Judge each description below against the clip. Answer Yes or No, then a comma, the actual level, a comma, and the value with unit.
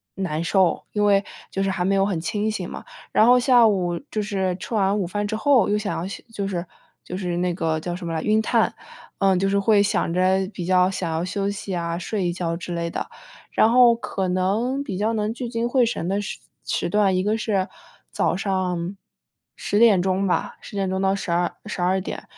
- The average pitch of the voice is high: Yes, high, 195 Hz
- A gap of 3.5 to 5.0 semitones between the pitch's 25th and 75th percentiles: No, average, 2.7 semitones